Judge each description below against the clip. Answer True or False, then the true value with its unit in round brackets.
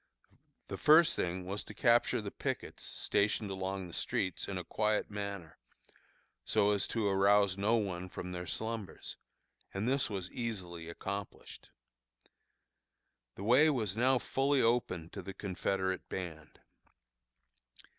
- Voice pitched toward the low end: True (100 Hz)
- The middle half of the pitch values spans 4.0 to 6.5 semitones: False (3.3 semitones)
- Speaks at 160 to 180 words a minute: False (135 wpm)